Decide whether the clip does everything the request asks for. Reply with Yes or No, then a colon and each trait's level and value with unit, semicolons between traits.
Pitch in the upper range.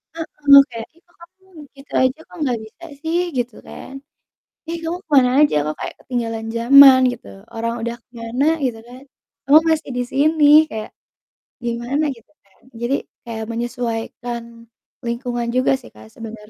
Yes: high, 245 Hz